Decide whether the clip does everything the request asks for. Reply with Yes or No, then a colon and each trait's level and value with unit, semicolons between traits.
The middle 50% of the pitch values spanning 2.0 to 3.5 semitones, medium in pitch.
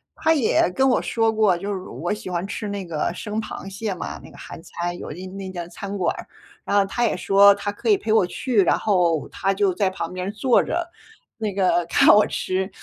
No: average, 2.8 semitones; high, 195 Hz